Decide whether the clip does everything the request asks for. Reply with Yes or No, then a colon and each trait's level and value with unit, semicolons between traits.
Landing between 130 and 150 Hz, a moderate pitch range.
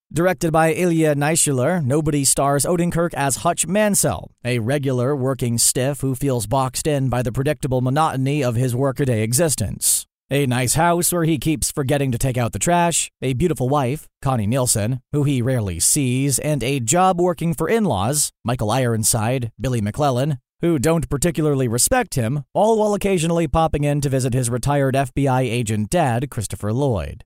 Yes: medium, 140 Hz; average, 4.2 semitones